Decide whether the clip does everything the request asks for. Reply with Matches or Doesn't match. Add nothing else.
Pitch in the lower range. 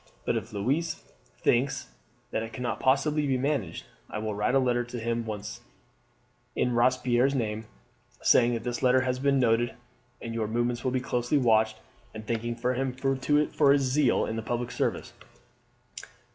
Matches